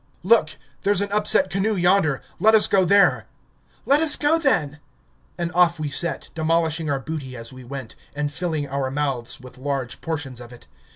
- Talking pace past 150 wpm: Yes, average, 180 wpm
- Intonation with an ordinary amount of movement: No, wide, 6.0 semitones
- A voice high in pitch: No, medium, 160 Hz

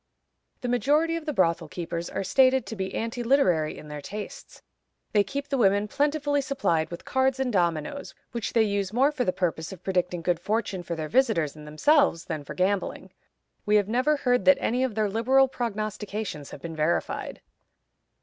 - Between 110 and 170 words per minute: No, average, 190 wpm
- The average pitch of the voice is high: Yes, high, 210 Hz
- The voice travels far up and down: Yes, wide, 7.3 semitones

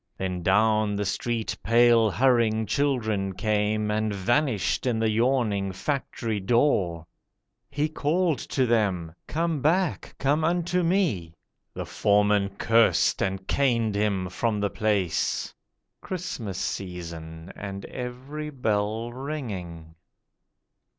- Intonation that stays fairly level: No, average, 5.2 semitones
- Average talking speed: No, slow, 110 wpm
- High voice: No, low, 110 Hz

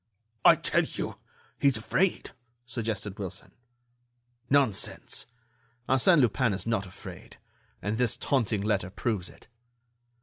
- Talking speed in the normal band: No, slow, 105 wpm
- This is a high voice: No, low, 110 Hz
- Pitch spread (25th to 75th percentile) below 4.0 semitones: No, average, 4.4 semitones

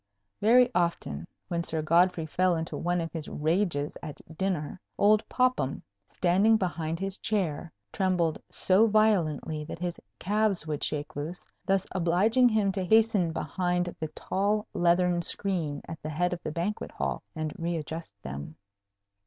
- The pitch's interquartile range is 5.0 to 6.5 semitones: No, average, 3.7 semitones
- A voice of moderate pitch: Yes, medium, 175 Hz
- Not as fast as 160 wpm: Yes, average, 150 wpm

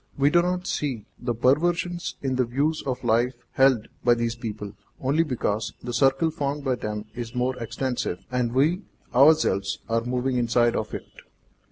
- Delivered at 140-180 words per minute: Yes, average, 170 wpm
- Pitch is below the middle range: Yes, low, 125 Hz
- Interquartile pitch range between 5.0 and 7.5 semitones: No, average, 3.2 semitones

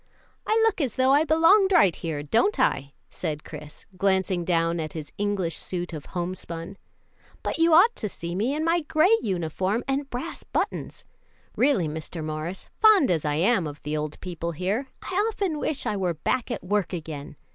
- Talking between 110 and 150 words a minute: No, average, 185 wpm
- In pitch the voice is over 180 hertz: Yes, high, 190 Hz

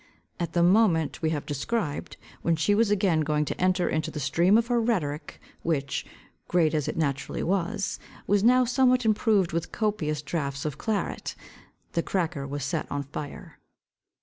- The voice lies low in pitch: No, medium, 170 Hz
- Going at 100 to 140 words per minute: No, average, 170 wpm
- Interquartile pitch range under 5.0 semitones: No, wide, 5.5 semitones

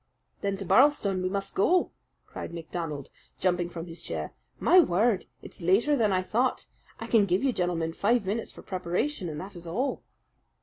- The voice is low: No, high, 190 Hz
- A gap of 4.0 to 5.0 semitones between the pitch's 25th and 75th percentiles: Yes, average, 4.7 semitones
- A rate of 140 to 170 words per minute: No, average, 180 wpm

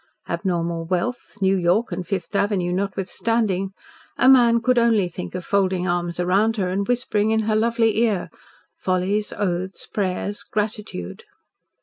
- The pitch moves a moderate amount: Yes, average, 3.5 semitones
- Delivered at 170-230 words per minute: No, average, 140 wpm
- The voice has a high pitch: Yes, high, 195 Hz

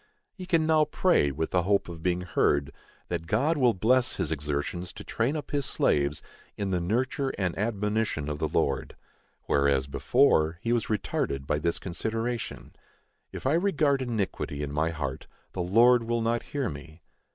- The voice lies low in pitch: Yes, low, 100 Hz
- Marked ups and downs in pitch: Yes, wide, 7.9 semitones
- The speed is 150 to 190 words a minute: Yes, average, 170 wpm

